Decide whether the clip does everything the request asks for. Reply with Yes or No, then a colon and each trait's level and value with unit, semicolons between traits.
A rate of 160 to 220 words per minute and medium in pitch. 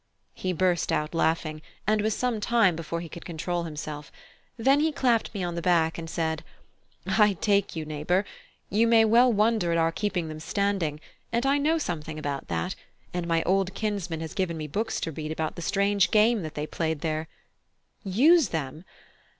Yes: average, 190 wpm; medium, 175 Hz